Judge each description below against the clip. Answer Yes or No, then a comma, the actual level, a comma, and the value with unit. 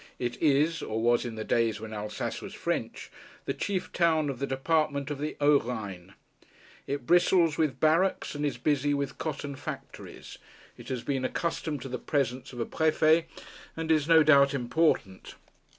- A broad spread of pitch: No, average, 4.3 semitones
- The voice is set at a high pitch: No, medium, 140 Hz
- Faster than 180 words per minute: No, average, 175 wpm